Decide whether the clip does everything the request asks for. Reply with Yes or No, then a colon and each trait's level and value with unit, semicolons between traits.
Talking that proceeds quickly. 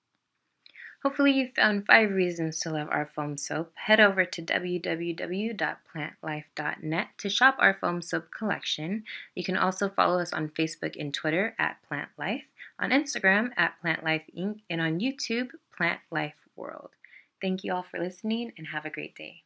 No: average, 165 wpm